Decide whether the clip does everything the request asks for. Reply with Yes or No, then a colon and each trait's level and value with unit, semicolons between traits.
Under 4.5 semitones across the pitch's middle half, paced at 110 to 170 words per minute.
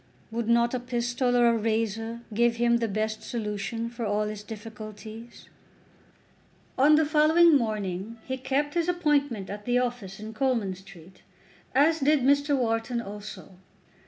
Yes: average, 3.5 semitones; average, 150 wpm